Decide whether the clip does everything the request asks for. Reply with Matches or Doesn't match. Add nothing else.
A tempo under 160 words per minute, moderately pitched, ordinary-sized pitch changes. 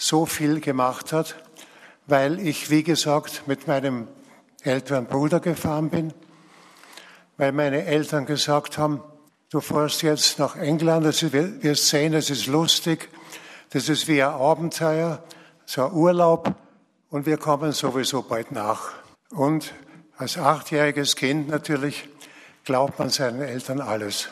Doesn't match